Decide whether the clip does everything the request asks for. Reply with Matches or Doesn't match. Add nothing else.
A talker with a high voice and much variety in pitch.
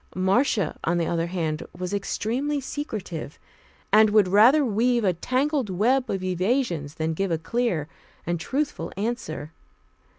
Matches